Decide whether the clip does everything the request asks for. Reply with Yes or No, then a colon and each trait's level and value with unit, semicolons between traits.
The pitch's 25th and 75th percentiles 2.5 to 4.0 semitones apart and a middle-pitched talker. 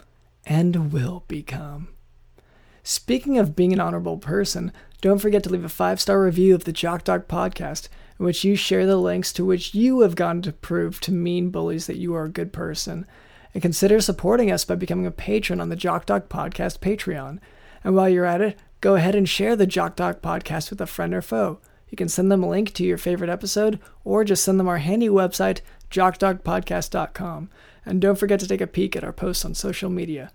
Yes: average, 2.8 semitones; medium, 180 Hz